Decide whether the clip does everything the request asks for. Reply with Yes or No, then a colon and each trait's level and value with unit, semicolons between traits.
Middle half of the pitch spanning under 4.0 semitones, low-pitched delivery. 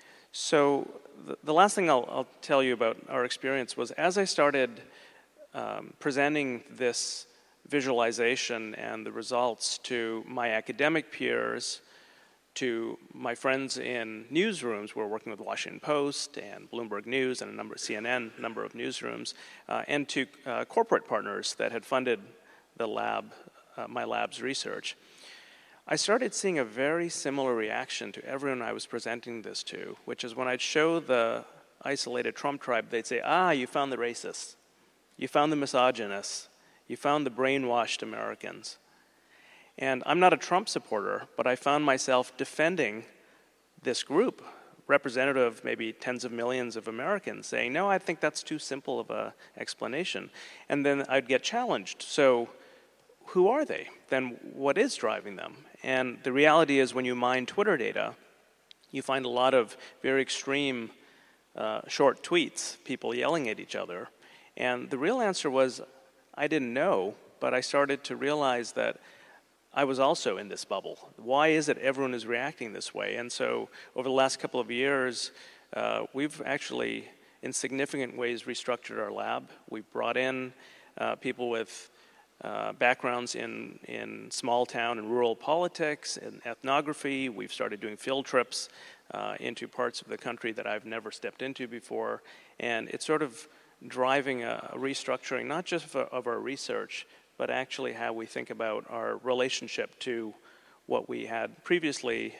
Yes: average, 2.7 semitones; low, 130 Hz